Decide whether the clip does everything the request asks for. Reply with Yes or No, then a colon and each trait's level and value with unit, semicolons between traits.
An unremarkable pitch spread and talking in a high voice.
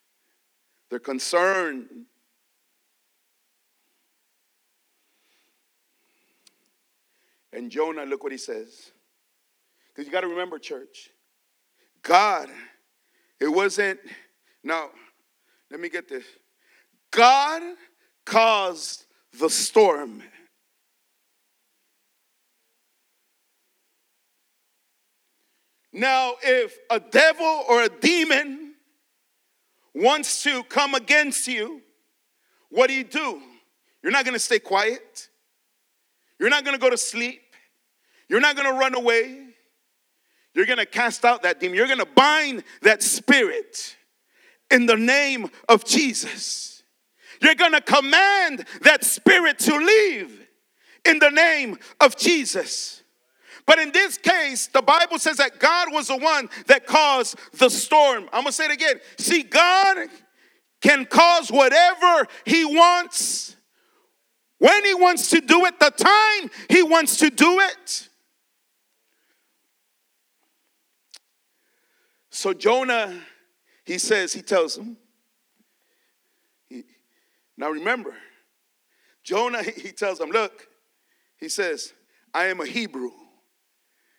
No: wide, 6.9 semitones; very high, 300 Hz